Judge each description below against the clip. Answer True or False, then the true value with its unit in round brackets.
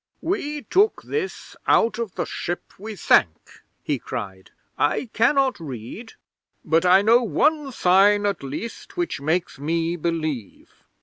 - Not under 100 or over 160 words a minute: True (135 wpm)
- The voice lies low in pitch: False (190 Hz)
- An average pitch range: False (7.7 semitones)